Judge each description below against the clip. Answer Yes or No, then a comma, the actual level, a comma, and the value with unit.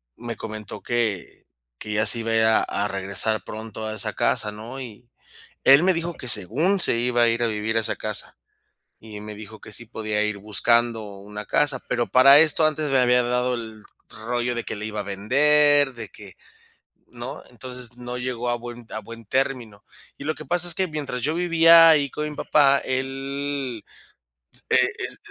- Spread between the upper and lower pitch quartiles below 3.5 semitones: No, average, 4.2 semitones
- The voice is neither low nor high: No, low, 120 Hz